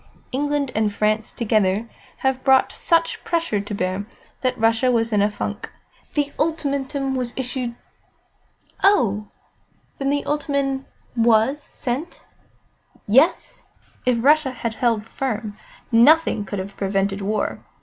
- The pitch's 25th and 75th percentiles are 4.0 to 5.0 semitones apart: Yes, average, 4.7 semitones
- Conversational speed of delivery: No, slow, 130 wpm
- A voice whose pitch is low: No, high, 245 Hz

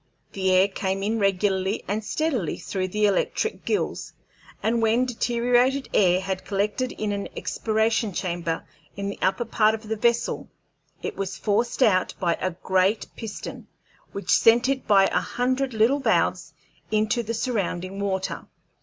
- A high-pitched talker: Yes, high, 210 Hz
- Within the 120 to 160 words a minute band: Yes, average, 155 wpm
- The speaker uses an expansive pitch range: No, average, 3.5 semitones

